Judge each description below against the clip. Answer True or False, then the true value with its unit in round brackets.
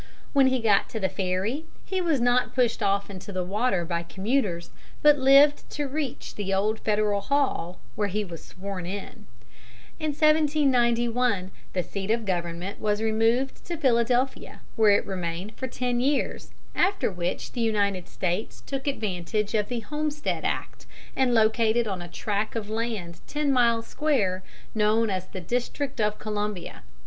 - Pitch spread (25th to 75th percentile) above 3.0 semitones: True (4.9 semitones)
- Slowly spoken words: False (160 wpm)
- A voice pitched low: False (220 Hz)